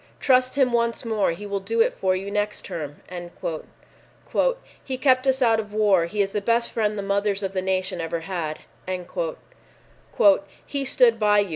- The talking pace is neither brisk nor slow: Yes, average, 175 wpm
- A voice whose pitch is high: Yes, high, 210 Hz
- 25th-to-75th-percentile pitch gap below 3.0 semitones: No, average, 3.4 semitones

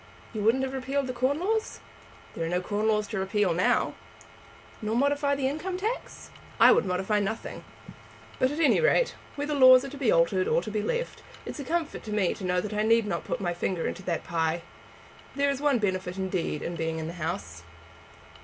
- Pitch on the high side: Yes, high, 215 Hz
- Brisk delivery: Yes, fast, 210 wpm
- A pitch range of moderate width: No, wide, 7.4 semitones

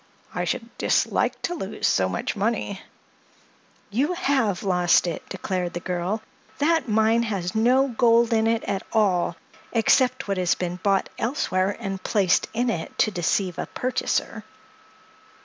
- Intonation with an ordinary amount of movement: Yes, average, 4.3 semitones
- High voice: Yes, high, 210 Hz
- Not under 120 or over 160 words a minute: Yes, average, 145 wpm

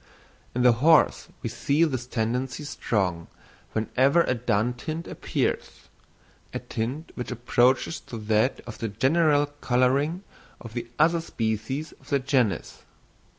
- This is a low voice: Yes, low, 125 Hz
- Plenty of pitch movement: No, average, 4.2 semitones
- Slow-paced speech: Yes, slow, 130 wpm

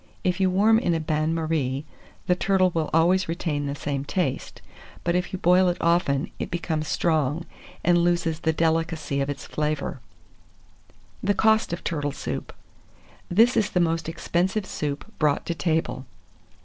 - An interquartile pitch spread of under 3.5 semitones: Yes, average, 2.9 semitones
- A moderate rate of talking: Yes, average, 160 wpm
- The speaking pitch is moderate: Yes, medium, 165 Hz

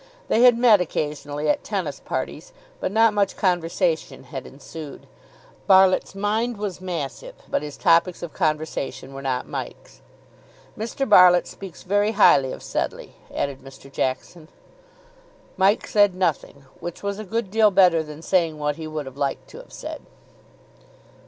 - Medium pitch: Yes, medium, 175 Hz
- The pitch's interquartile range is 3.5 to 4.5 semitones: No, wide, 5.5 semitones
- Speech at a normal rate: Yes, average, 150 wpm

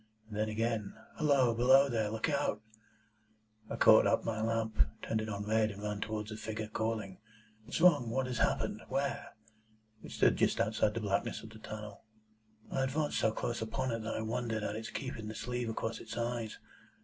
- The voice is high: No, low, 110 Hz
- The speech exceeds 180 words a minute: Yes, average, 195 wpm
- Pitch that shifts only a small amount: Yes, narrow, 1.9 semitones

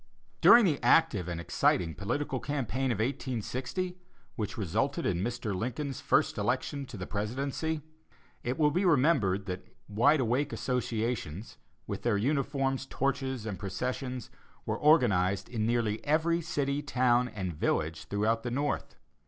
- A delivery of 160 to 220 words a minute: No, average, 140 wpm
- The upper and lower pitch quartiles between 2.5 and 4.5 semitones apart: No, average, 5.2 semitones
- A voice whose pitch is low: Yes, low, 125 Hz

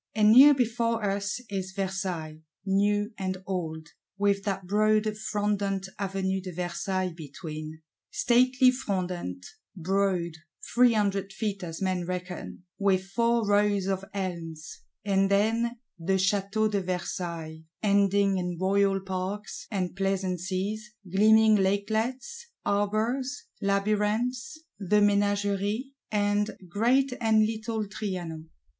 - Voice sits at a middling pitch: No, high, 200 Hz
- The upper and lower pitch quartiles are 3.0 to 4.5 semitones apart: No, narrow, 2.4 semitones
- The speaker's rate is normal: No, slow, 110 wpm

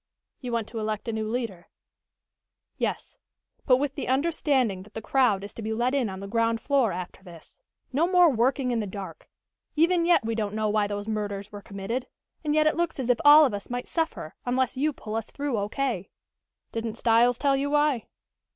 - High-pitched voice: Yes, high, 235 Hz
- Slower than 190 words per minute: No, fast, 205 wpm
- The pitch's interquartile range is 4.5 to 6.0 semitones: Yes, average, 4.8 semitones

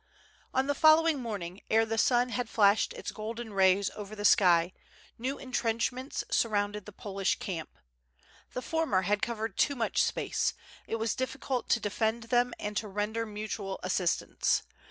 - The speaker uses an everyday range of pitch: Yes, average, 3.2 semitones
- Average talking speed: Yes, average, 160 wpm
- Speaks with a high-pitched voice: Yes, high, 220 Hz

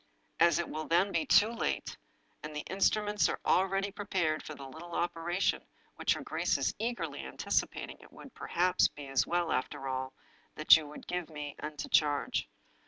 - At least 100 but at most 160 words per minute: No, average, 175 wpm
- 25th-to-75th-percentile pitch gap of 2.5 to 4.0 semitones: No, average, 4.4 semitones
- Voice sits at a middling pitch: Yes, medium, 170 Hz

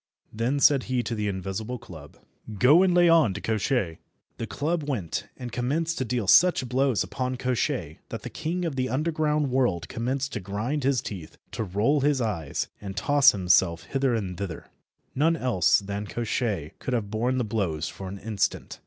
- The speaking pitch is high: No, low, 120 Hz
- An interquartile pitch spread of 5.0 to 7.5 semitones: Yes, wide, 5.6 semitones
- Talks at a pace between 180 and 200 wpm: Yes, average, 185 wpm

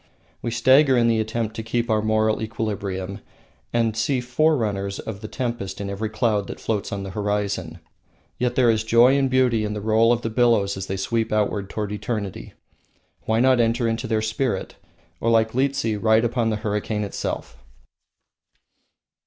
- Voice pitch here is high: No, low, 110 Hz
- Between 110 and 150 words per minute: No, average, 170 wpm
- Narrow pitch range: Yes, narrow, 2.3 semitones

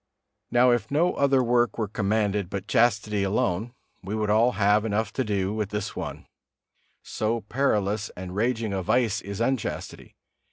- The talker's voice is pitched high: No, low, 110 Hz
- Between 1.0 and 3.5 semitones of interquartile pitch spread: Yes, average, 3.0 semitones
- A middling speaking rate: Yes, average, 160 wpm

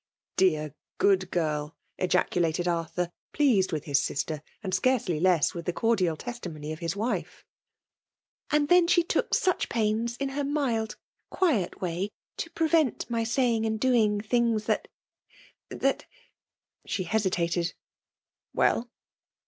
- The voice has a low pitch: No, high, 205 Hz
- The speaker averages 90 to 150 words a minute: Yes, average, 140 wpm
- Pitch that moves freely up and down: Yes, wide, 6.0 semitones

